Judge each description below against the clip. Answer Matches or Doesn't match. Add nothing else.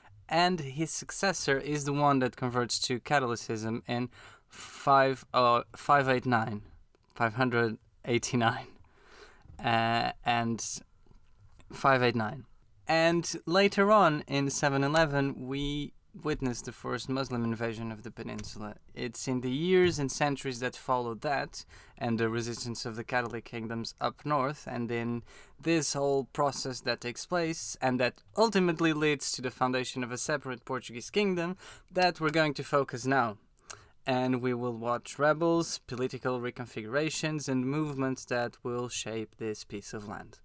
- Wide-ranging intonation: Doesn't match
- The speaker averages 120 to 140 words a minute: Matches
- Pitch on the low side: Matches